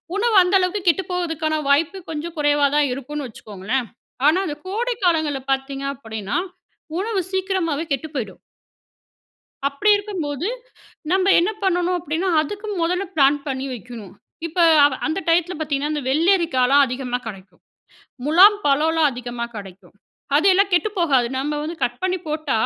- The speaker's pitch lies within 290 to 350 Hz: Yes, very high, 305 Hz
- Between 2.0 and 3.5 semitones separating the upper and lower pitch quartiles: No, average, 5.2 semitones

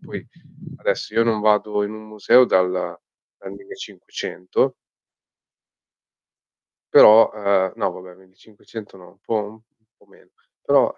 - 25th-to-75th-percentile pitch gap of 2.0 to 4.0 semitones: Yes, narrow, 2.5 semitones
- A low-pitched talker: Yes, low, 105 Hz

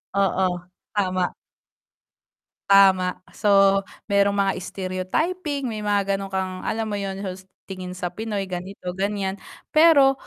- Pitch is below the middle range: No, high, 195 Hz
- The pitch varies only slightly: Yes, narrow, 1.8 semitones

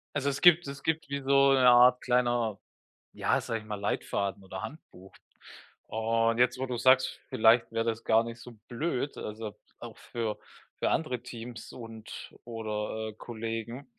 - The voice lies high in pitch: No, low, 115 Hz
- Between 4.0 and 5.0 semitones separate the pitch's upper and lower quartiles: No, narrow, 2.6 semitones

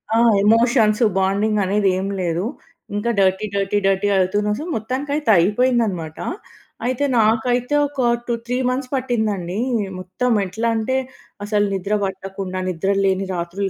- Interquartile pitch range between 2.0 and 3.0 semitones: No, average, 3.8 semitones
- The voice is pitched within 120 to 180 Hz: No, high, 205 Hz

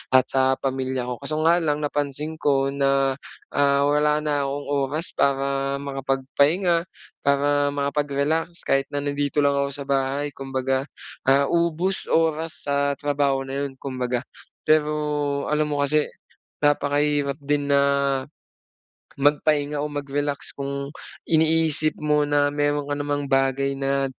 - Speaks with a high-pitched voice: No, medium, 145 Hz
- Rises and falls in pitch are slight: Yes, narrow, 1.3 semitones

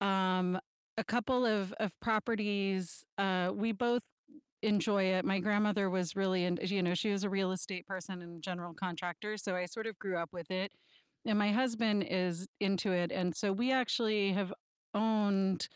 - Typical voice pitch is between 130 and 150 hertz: No, high, 195 Hz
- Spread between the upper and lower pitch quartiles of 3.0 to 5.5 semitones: No, narrow, 2.5 semitones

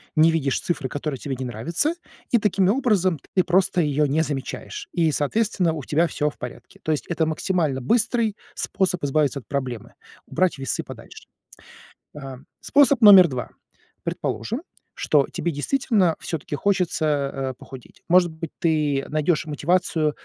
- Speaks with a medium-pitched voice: Yes, medium, 160 Hz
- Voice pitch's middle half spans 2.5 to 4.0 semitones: No, average, 4.5 semitones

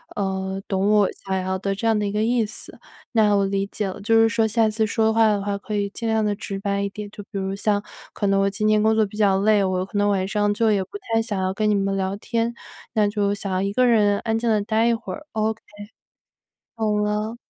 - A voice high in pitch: Yes, high, 210 Hz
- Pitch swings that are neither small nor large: No, narrow, 1.9 semitones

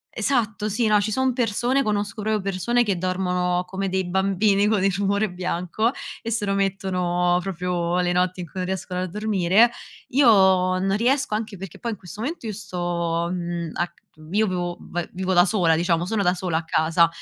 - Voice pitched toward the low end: No, high, 190 Hz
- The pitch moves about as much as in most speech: Yes, average, 3.0 semitones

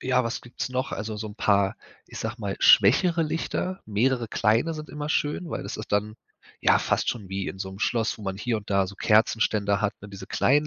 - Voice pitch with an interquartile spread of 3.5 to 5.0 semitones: Yes, average, 4.2 semitones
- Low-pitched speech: Yes, low, 110 Hz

